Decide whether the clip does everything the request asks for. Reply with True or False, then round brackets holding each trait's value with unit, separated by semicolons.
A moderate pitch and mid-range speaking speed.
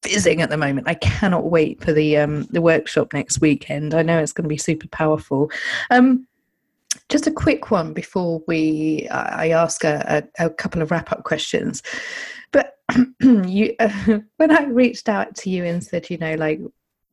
True (170 Hz; 180 wpm)